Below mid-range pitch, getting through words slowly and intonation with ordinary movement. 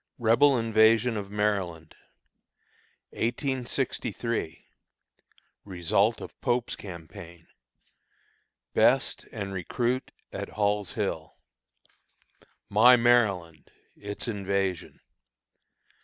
Yes: low, 105 Hz; slow, 70 wpm; average, 3.8 semitones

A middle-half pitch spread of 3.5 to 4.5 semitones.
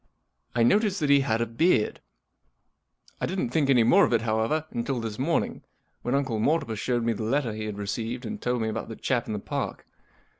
Yes: average, 4.1 semitones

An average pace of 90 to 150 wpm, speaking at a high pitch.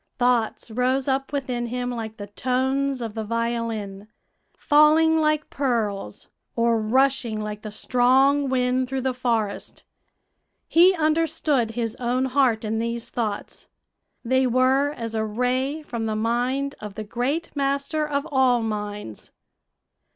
Yes: slow, 135 wpm; very high, 250 Hz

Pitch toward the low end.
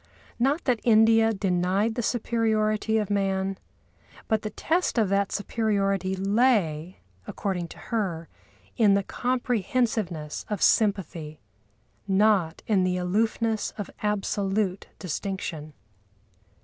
No: high, 205 Hz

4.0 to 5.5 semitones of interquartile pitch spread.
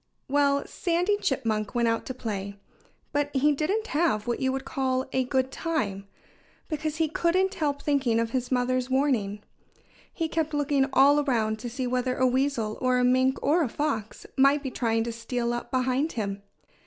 No: average, 3.6 semitones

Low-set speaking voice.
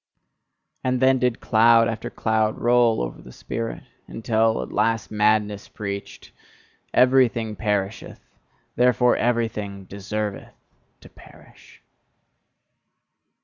Yes: low, 110 Hz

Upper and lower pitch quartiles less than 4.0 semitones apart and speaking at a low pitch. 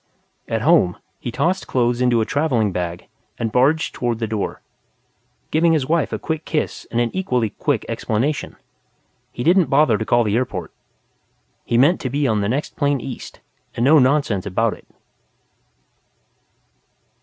No: average, 5.0 semitones; low, 125 Hz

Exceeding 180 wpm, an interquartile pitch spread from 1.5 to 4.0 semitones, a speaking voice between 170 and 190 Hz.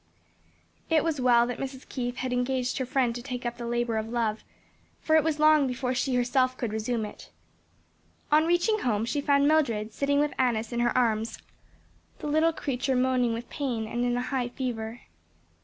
No: average, 190 wpm; average, 2.9 semitones; very high, 250 Hz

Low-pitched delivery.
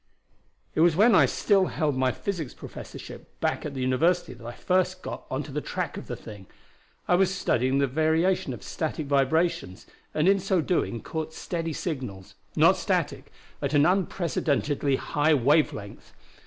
No: medium, 155 Hz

